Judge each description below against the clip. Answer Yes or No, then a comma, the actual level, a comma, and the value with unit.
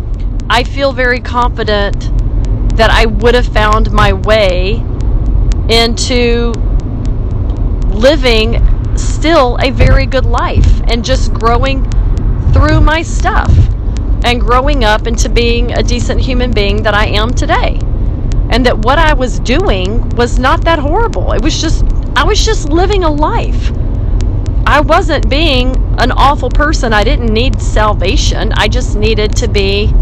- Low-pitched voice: Yes, low, 105 Hz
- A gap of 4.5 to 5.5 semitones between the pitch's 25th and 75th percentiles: No, narrow, 2.5 semitones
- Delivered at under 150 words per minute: Yes, average, 140 wpm